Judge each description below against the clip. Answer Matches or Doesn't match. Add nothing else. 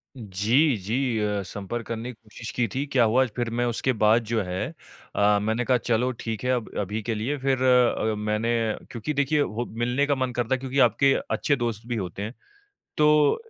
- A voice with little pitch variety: Doesn't match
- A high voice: Doesn't match